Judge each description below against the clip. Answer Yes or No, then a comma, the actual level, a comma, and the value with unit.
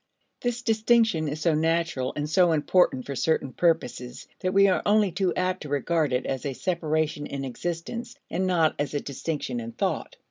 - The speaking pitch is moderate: Yes, medium, 160 Hz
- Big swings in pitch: No, average, 4.5 semitones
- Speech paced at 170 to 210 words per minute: Yes, average, 185 wpm